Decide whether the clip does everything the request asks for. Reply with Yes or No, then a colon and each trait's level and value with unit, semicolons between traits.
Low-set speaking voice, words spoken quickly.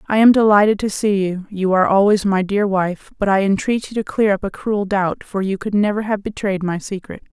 No: high, 200 Hz; fast, 245 wpm